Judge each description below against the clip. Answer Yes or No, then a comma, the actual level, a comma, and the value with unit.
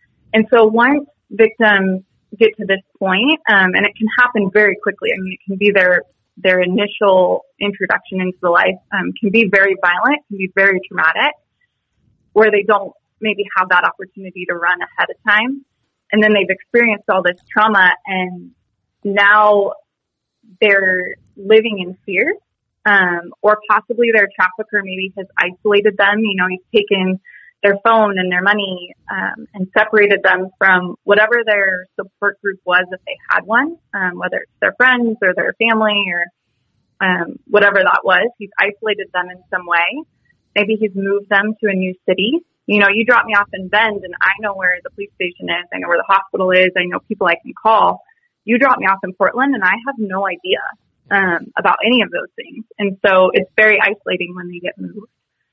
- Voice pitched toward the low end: No, high, 200 Hz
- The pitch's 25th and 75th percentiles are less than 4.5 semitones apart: Yes, average, 2.8 semitones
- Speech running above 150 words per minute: Yes, average, 190 wpm